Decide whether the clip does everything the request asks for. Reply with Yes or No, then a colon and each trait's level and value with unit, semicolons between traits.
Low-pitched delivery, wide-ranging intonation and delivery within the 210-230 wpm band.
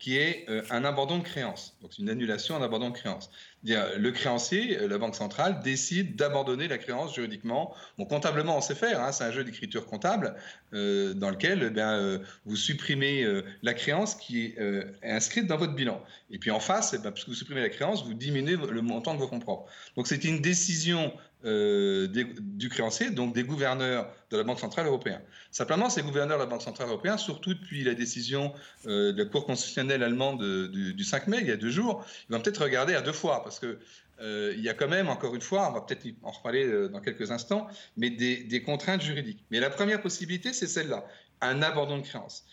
No: medium, 145 Hz; wide, 7.9 semitones; fast, 220 wpm